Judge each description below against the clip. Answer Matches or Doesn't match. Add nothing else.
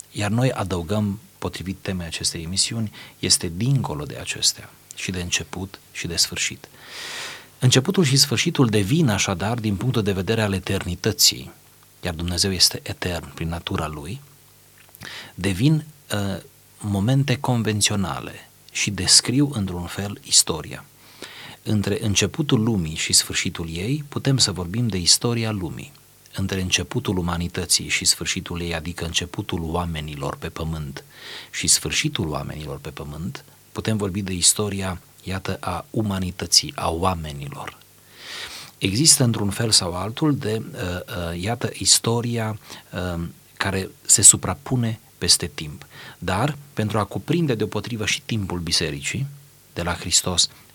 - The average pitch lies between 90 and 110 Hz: Matches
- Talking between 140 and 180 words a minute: Doesn't match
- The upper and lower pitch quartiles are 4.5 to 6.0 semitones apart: Matches